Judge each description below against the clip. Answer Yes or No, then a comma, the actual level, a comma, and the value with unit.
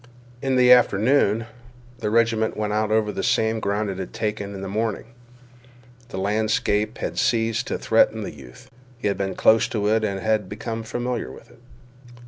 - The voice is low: Yes, low, 110 Hz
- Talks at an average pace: Yes, average, 175 wpm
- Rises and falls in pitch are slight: Yes, narrow, 1.7 semitones